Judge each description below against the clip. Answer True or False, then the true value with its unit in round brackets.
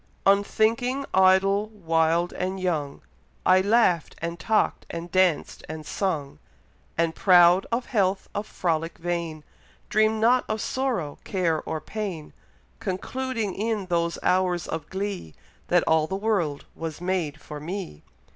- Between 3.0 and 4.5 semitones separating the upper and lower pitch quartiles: True (4.0 semitones)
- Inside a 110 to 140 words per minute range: True (135 wpm)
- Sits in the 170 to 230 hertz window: True (185 Hz)